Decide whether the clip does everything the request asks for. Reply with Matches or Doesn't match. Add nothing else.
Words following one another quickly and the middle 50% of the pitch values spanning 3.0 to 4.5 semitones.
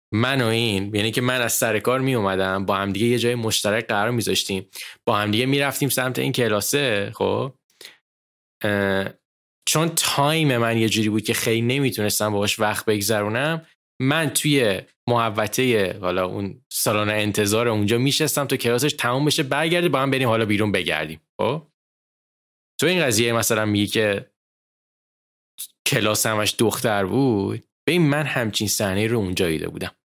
Matches